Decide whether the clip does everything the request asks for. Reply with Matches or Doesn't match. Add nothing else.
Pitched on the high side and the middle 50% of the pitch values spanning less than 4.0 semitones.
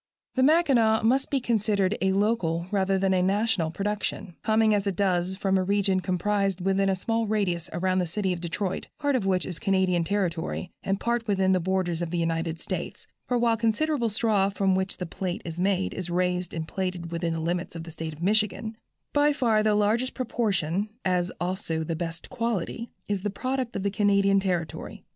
Matches